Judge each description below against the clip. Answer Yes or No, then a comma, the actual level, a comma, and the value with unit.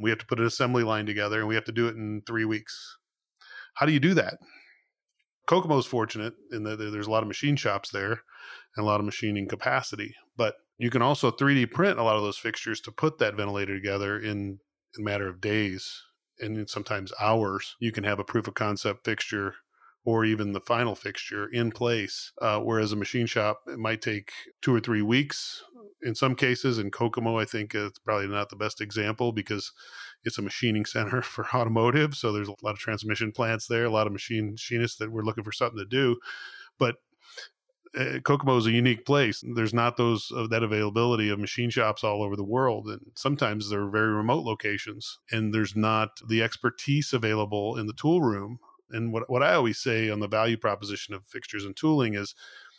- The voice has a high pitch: No, low, 110 Hz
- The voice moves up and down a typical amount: No, narrow, 2.2 semitones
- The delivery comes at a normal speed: No, fast, 210 wpm